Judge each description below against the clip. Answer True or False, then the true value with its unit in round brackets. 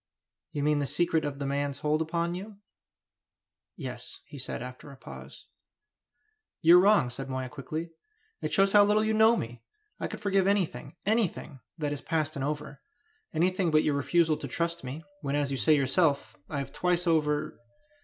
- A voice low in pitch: False (155 Hz)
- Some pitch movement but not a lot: True (4.0 semitones)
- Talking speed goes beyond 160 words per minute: True (185 wpm)